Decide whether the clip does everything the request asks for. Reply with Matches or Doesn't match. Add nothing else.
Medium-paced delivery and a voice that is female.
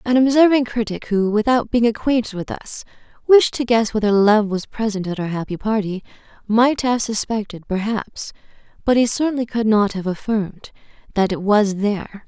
Matches